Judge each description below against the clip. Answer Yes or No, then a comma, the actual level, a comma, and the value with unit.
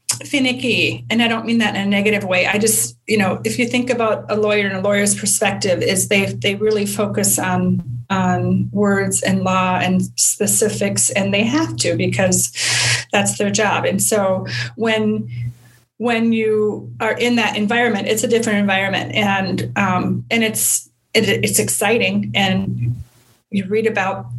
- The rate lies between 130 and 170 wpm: Yes, average, 165 wpm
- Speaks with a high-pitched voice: Yes, high, 200 Hz